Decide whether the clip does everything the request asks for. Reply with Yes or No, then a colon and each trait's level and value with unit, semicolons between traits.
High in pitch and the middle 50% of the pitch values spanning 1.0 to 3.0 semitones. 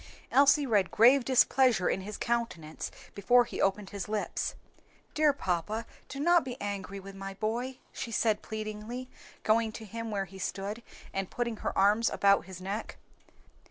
No: high, 215 Hz; average, 3.7 semitones